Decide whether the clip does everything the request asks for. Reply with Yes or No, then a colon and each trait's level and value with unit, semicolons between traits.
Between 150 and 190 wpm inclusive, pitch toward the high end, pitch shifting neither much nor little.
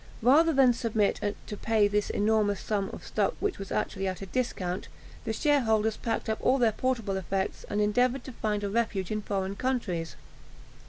Yes: average, 180 wpm; high, 215 Hz; average, 3.6 semitones